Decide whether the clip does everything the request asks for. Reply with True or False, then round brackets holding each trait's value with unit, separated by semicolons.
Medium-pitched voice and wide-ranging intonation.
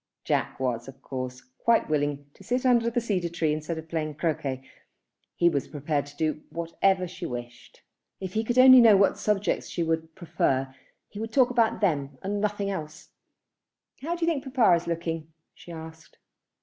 True (170 Hz; 5.9 semitones)